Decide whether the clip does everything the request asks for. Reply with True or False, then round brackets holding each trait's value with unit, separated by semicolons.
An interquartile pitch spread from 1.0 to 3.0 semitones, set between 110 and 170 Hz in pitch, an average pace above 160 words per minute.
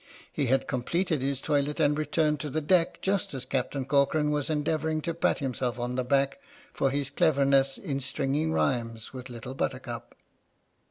True (2.5 semitones; 140 Hz; 170 wpm)